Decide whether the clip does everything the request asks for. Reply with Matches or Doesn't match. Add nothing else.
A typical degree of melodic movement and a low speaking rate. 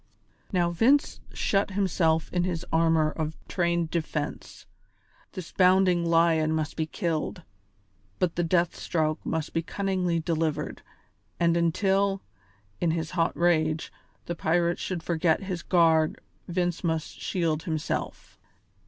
Doesn't match